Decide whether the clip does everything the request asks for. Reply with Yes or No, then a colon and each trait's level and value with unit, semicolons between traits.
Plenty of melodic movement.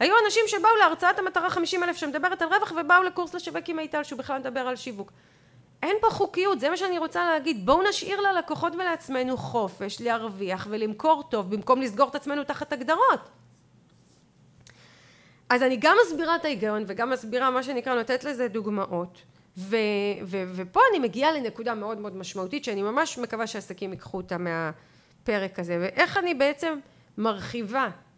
Yes: wide, 7.9 semitones